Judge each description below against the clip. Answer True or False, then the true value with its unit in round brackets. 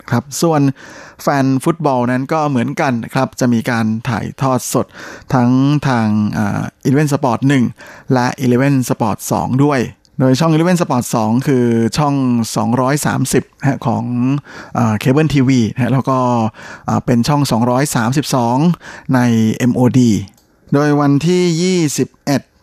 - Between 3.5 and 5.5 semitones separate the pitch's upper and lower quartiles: False (3.0 semitones)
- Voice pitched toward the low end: True (130 Hz)